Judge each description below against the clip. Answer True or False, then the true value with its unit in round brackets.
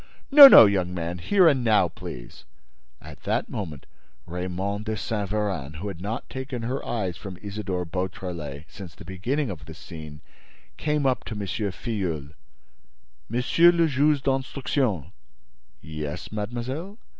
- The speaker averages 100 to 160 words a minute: True (145 wpm)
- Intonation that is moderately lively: False (6.5 semitones)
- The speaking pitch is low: True (100 Hz)